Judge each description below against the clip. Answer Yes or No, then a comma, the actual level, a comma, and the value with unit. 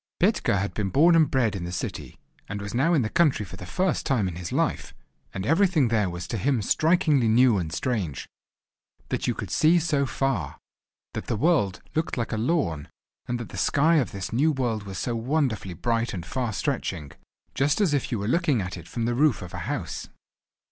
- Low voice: Yes, low, 120 Hz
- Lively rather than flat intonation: Yes, wide, 7.1 semitones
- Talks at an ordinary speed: No, fast, 210 wpm